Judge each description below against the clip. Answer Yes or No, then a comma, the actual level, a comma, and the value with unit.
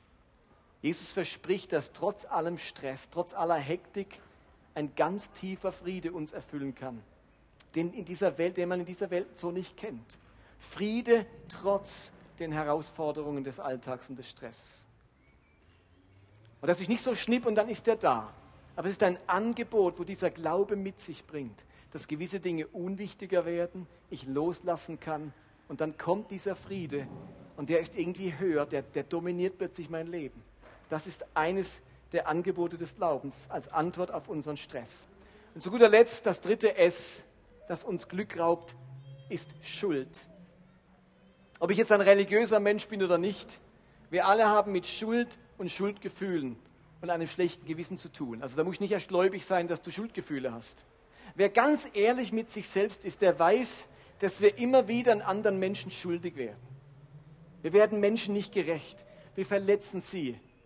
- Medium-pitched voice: Yes, medium, 175 Hz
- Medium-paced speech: Yes, average, 165 wpm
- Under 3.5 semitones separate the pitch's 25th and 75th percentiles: No, average, 4.7 semitones